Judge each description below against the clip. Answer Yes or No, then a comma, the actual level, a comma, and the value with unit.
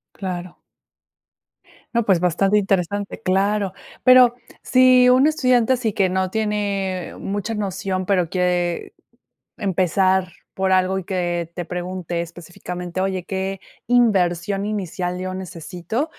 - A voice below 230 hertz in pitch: Yes, high, 190 Hz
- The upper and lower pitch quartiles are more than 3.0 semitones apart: No, narrow, 2.6 semitones